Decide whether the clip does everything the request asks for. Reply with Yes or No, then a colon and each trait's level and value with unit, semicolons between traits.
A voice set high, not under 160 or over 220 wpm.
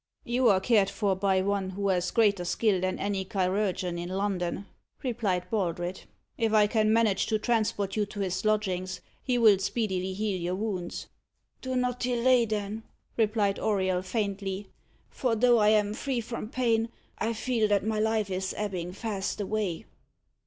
Yes: high, 205 Hz; average, 165 wpm